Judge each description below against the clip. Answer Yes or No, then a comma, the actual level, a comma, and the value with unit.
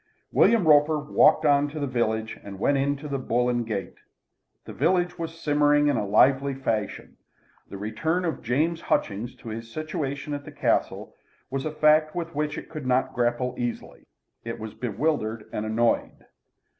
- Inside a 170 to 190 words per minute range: Yes, average, 175 wpm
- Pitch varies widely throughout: No, average, 4.7 semitones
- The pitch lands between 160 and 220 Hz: No, medium, 140 Hz